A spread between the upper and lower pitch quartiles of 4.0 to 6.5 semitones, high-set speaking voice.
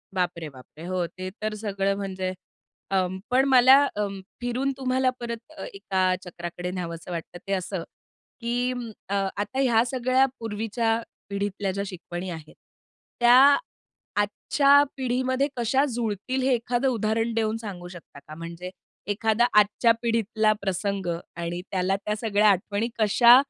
Yes: average, 4.4 semitones; high, 210 Hz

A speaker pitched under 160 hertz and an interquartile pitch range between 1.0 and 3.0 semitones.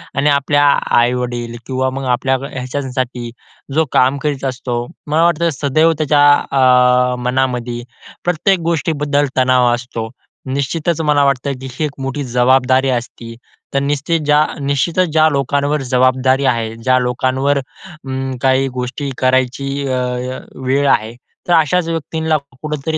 Yes: low, 135 Hz; average, 2.7 semitones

